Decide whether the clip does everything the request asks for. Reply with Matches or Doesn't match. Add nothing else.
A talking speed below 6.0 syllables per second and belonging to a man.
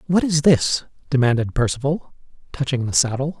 Matches